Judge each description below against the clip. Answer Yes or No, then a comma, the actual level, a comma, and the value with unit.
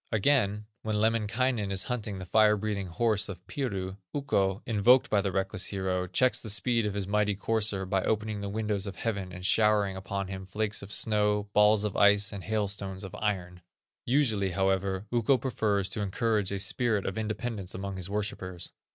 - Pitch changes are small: Yes, narrow, 2.2 semitones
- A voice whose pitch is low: Yes, low, 105 Hz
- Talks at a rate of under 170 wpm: No, average, 180 wpm